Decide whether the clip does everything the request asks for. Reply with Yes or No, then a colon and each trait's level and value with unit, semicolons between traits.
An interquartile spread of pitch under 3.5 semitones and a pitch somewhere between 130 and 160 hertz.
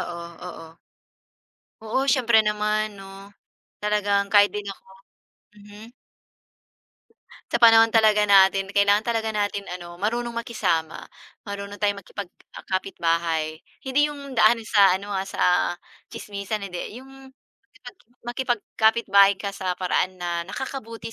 No: average, 2.7 semitones; high, 205 Hz